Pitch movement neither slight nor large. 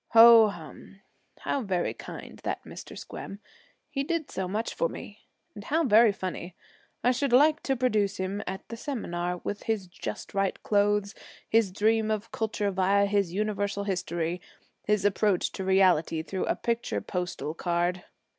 Yes: average, 3.3 semitones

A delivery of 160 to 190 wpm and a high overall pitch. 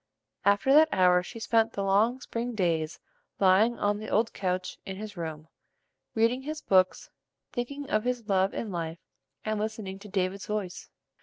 Yes: average, 165 wpm; high, 205 Hz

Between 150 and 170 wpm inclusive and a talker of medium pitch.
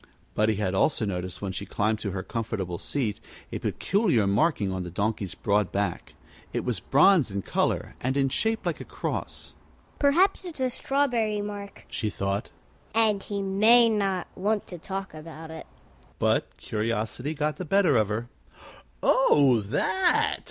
Yes: average, 160 wpm; medium, 145 Hz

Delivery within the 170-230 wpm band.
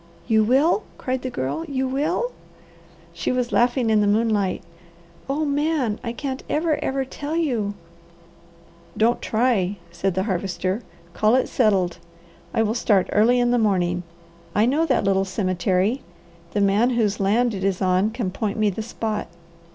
No: average, 160 wpm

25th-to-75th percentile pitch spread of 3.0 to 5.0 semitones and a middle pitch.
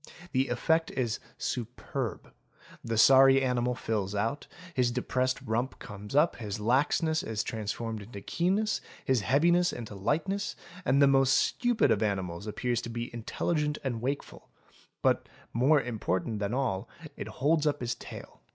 No: average, 4.5 semitones; low, 125 Hz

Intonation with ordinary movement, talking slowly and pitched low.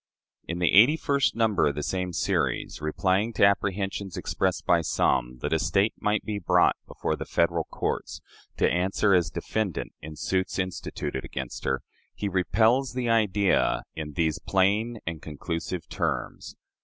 No: average, 4.0 semitones; average, 155 wpm; very low, 95 Hz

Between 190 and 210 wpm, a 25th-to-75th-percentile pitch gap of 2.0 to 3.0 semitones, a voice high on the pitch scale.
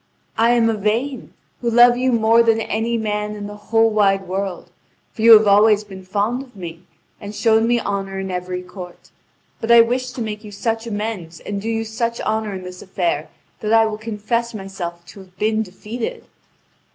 Yes: average, 195 wpm; average, 2.7 semitones; high, 215 Hz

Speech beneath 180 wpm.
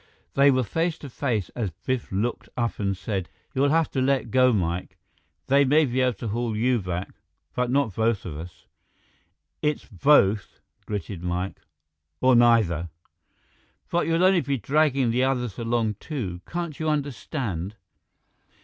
Yes: average, 155 wpm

